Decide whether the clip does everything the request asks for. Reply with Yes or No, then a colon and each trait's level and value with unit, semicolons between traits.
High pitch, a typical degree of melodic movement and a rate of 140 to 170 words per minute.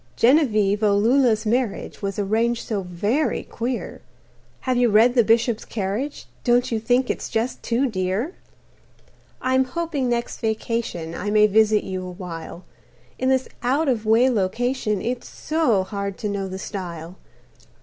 Yes: high, 225 Hz; average, 3.8 semitones; average, 155 wpm